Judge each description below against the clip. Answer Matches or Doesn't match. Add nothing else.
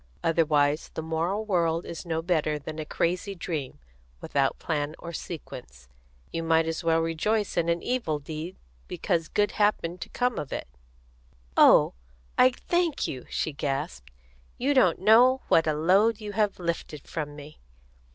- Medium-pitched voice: Matches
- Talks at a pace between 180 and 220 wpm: Doesn't match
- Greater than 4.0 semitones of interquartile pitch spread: Matches